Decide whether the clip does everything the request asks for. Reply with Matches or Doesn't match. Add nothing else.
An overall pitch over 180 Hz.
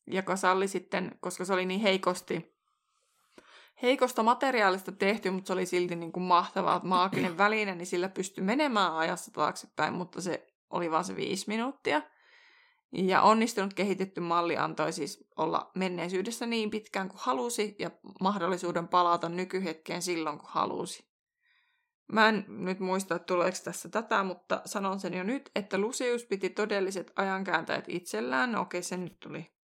Matches